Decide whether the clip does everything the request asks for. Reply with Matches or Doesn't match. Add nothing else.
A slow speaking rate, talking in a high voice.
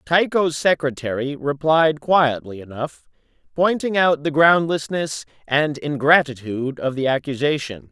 Doesn't match